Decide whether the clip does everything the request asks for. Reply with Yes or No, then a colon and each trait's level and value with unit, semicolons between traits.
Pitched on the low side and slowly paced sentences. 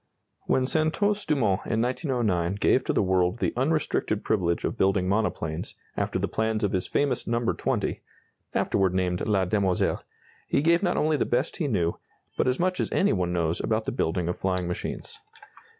No: low, 110 Hz; average, 180 wpm